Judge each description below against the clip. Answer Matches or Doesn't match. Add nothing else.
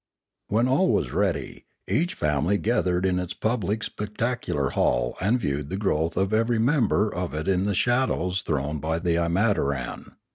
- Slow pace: Doesn't match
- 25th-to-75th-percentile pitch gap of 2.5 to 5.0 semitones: Doesn't match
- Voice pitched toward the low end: Matches